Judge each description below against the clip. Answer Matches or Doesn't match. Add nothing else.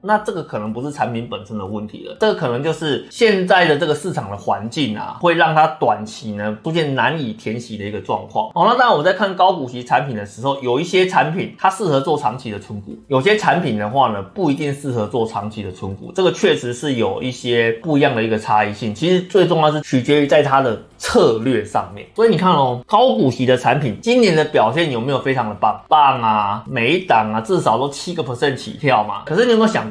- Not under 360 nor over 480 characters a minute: Matches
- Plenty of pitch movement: Matches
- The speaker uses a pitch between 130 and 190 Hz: Matches